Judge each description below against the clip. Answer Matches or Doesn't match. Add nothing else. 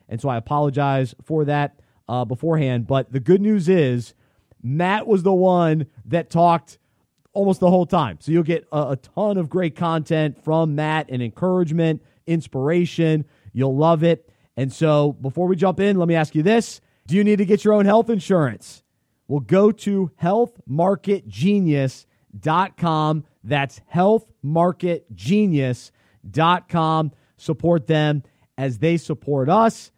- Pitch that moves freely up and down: Doesn't match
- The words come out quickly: Doesn't match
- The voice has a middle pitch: Matches